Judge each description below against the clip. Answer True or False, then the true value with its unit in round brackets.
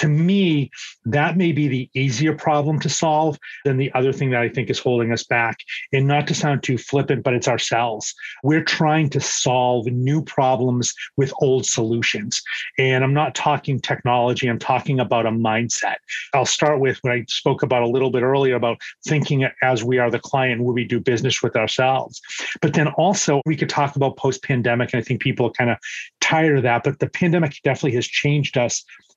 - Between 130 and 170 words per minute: False (205 wpm)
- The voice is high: False (130 Hz)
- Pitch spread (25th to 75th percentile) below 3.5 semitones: True (2.9 semitones)